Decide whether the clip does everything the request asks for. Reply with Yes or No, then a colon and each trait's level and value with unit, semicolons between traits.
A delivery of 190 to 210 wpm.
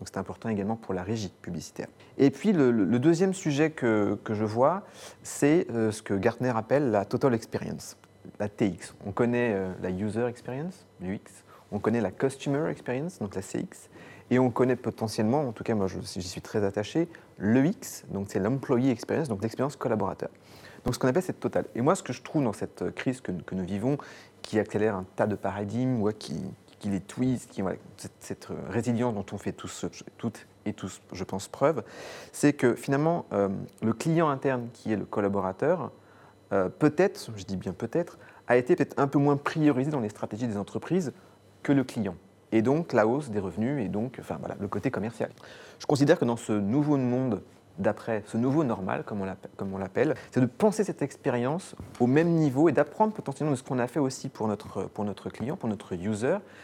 Yes: average, 205 wpm